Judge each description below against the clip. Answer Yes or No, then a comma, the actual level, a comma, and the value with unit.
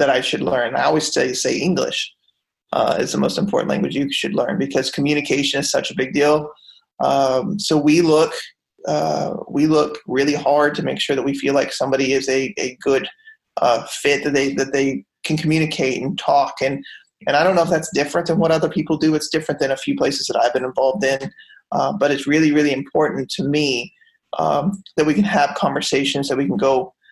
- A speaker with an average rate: No, fast, 215 wpm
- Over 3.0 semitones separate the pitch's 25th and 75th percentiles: No, narrow, 2.6 semitones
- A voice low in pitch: No, medium, 145 Hz